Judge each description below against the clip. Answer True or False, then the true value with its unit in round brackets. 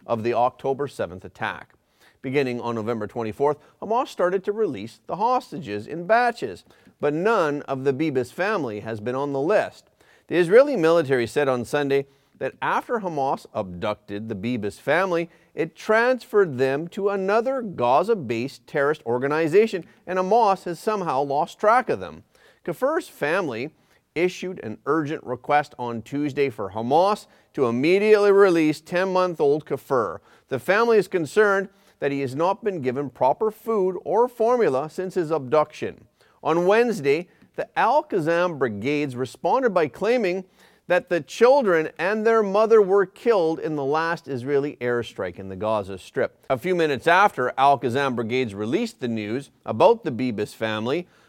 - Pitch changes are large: True (7.5 semitones)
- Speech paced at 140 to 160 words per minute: True (155 wpm)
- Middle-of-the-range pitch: True (155 Hz)